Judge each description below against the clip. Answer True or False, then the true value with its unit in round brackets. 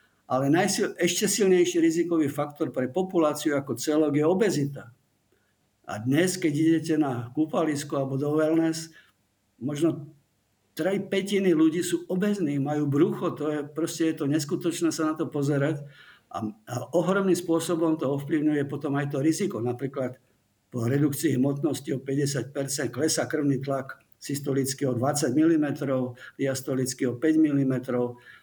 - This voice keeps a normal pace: True (140 wpm)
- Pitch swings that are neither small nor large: True (3.2 semitones)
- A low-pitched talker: False (150 Hz)